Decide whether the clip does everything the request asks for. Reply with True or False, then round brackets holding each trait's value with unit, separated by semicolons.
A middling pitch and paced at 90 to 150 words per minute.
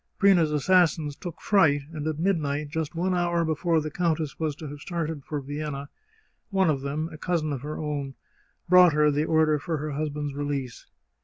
False (155 Hz; 185 wpm)